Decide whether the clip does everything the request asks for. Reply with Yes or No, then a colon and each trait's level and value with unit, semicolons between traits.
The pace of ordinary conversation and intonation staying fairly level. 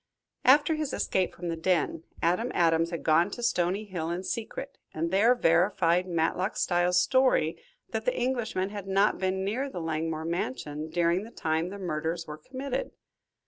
No: average, 170 wpm; average, 4.6 semitones